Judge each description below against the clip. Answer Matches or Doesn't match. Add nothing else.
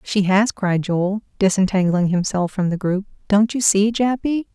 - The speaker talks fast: Doesn't match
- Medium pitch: Doesn't match